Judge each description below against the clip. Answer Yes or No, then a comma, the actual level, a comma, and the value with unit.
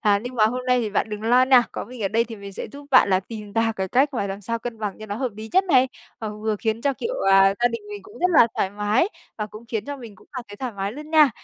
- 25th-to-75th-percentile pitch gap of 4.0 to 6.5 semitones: No, average, 3.6 semitones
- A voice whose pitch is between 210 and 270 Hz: Yes, high, 225 Hz